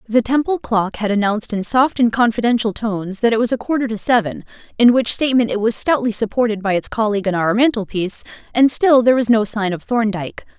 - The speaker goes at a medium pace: No, fast, 215 wpm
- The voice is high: Yes, high, 225 Hz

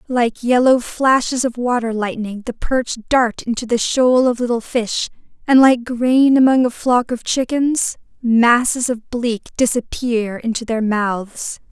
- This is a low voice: No, high, 240 Hz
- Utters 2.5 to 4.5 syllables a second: Yes, 4.0 syllables/s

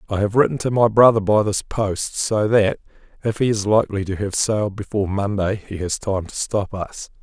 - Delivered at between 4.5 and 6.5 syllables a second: Yes, 5.3 syllables/s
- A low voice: Yes, low, 105 Hz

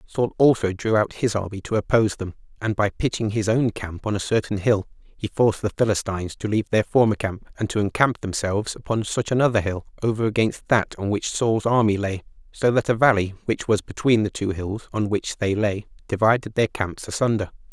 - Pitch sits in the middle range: No, low, 105 Hz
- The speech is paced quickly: Yes, fast, 210 wpm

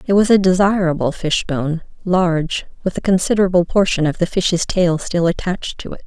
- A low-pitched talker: No, medium, 180 Hz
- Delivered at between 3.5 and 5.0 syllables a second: No, 5.6 syllables/s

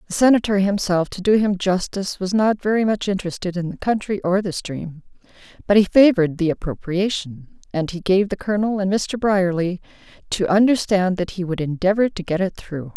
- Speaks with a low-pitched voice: No, high, 190 Hz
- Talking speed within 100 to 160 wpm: No, average, 190 wpm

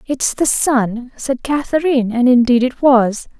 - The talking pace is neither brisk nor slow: Yes, average, 160 wpm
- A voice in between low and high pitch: No, very high, 255 Hz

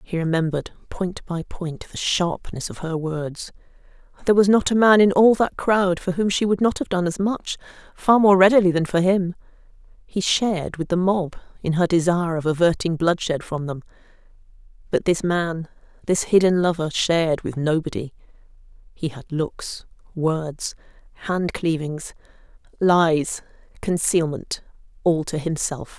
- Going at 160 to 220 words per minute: No, average, 150 wpm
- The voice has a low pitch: No, medium, 175 Hz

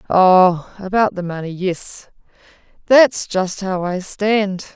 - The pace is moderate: No, slow, 115 wpm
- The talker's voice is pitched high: Yes, high, 195 Hz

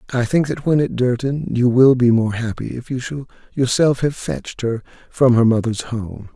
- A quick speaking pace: Yes, fast, 210 wpm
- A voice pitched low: Yes, low, 125 Hz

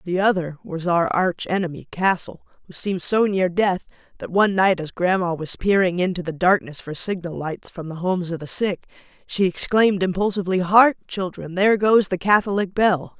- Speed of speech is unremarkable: Yes, average, 185 wpm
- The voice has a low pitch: No, medium, 185 Hz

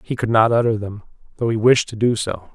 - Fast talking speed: Yes, fast, 260 wpm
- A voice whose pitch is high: No, low, 110 Hz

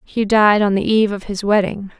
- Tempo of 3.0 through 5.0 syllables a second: No, 5.4 syllables/s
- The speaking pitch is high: Yes, high, 205 Hz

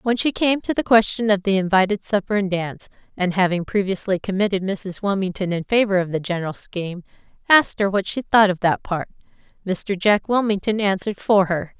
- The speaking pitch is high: Yes, high, 195 Hz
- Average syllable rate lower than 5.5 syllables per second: No, 5.7 syllables/s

